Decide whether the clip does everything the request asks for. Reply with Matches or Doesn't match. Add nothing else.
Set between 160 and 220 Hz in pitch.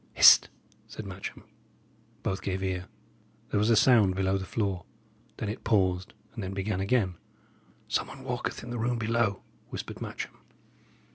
Doesn't match